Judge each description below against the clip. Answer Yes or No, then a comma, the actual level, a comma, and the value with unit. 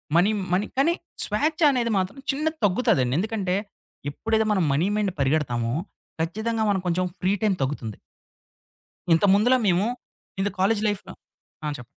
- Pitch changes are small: No, average, 4.9 semitones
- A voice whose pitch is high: Yes, high, 195 Hz